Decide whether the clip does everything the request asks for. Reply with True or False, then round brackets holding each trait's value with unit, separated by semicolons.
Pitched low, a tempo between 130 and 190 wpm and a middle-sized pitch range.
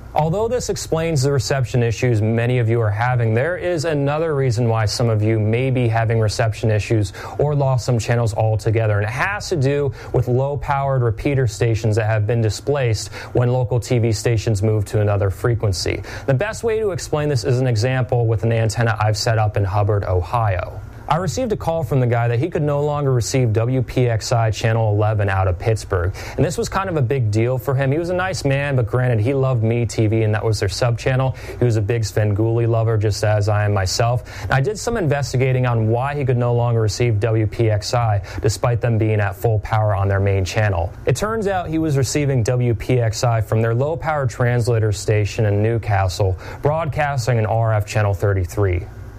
False (115 Hz; 205 wpm; 3.4 semitones)